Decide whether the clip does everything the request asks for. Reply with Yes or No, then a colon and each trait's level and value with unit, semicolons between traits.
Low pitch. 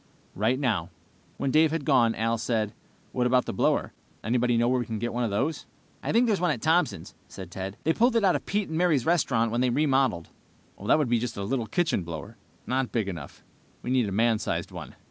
Yes: low, 125 Hz